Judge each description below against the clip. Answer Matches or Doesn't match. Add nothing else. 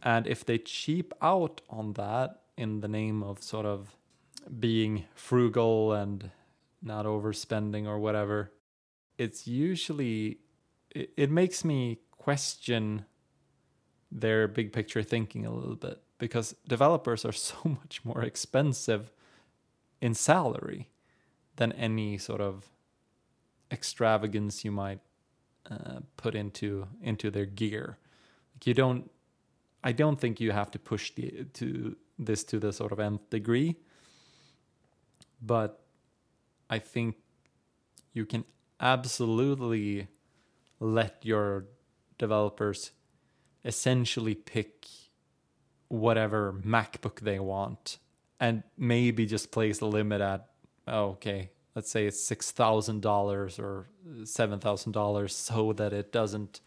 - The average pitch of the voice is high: Doesn't match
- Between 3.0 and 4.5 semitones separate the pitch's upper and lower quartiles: Doesn't match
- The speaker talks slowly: Matches